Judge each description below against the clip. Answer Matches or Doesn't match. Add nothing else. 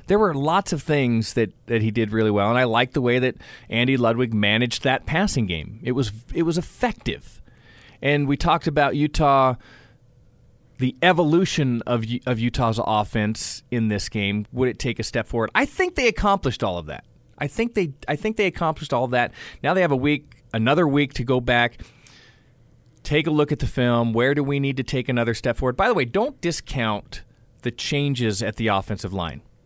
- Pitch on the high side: Doesn't match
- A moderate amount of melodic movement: Matches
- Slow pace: Doesn't match